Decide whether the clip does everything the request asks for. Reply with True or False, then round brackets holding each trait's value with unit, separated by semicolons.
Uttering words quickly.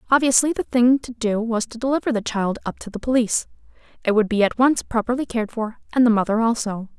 True (225 wpm)